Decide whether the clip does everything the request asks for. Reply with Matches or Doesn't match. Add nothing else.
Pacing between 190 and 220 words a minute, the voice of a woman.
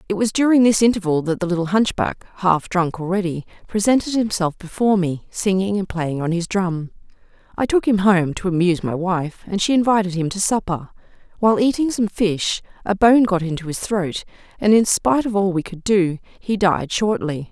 Matches